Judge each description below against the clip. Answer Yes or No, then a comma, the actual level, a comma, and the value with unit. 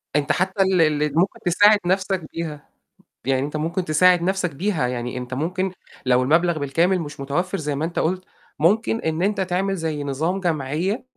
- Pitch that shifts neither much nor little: Yes, average, 4.2 semitones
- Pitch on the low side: No, medium, 170 Hz